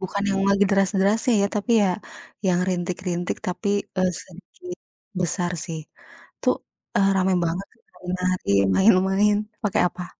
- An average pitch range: No, narrow, 1.8 semitones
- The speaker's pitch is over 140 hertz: Yes, high, 190 Hz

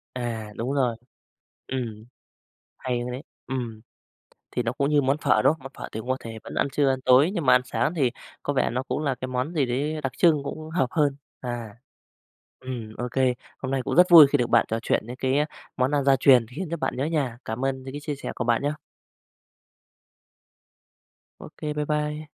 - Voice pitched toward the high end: No, low, 130 Hz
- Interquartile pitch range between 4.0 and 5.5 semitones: No, average, 2.9 semitones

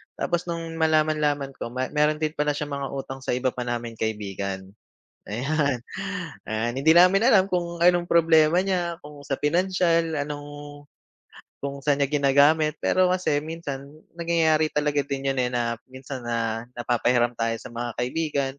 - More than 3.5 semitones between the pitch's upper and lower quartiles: Yes, average, 4.3 semitones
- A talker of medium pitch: Yes, medium, 145 Hz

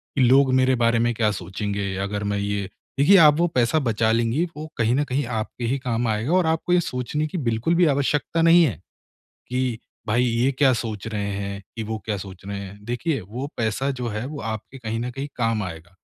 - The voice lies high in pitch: No, low, 120 Hz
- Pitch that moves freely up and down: No, average, 4.2 semitones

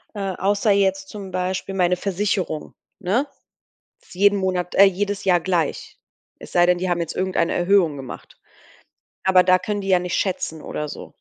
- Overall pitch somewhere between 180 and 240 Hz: Yes, medium, 185 Hz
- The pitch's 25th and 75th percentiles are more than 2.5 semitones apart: No, narrow, 1.8 semitones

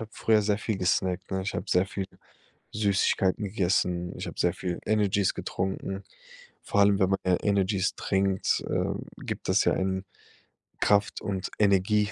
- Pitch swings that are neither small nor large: No, narrow, 1.5 semitones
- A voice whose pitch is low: Yes, very low, 95 Hz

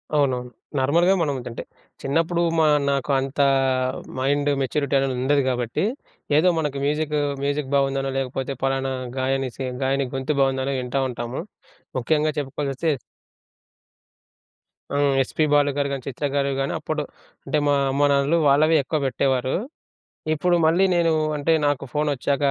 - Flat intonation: Yes, narrow, 2.0 semitones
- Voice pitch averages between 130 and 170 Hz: Yes, medium, 140 Hz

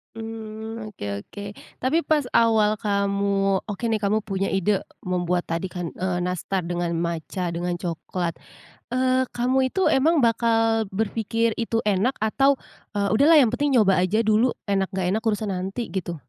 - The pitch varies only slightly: No, average, 3.8 semitones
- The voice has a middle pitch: No, high, 210 Hz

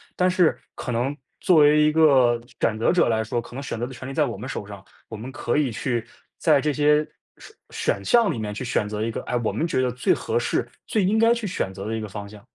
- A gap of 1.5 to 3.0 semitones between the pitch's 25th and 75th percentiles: No, wide, 5.5 semitones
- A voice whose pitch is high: No, low, 130 Hz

